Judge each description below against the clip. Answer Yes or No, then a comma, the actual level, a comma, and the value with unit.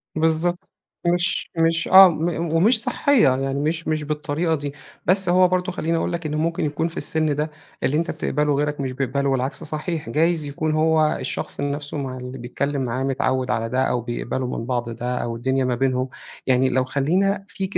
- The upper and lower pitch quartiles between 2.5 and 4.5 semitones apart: Yes, average, 3.9 semitones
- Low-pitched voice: No, medium, 150 Hz